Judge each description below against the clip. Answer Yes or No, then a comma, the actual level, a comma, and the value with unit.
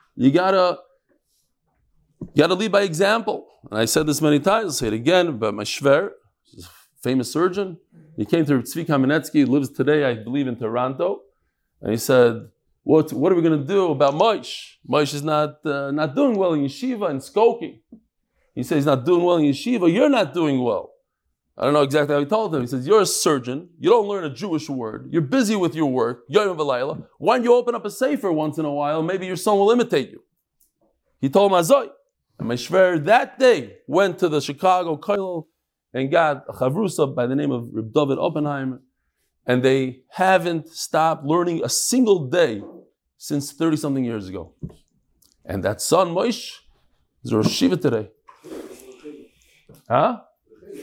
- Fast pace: No, average, 180 wpm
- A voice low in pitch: No, medium, 155 Hz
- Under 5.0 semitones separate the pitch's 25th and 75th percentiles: No, wide, 5.5 semitones